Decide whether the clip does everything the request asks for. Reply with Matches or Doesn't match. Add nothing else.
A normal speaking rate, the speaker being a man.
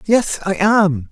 Matches